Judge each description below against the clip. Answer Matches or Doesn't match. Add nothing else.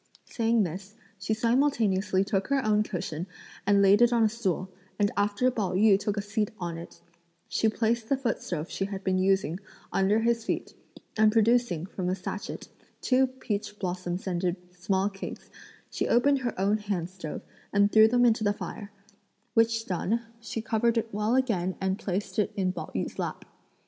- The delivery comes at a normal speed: Matches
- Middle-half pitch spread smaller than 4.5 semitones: Matches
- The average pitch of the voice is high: Matches